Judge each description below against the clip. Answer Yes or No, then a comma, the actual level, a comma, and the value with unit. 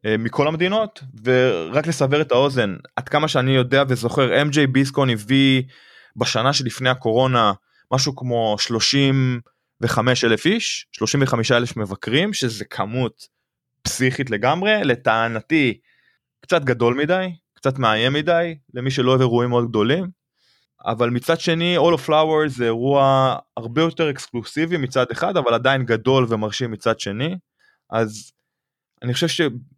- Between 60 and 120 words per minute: No, average, 130 wpm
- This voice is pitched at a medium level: No, low, 130 Hz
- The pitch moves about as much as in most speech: Yes, average, 4.1 semitones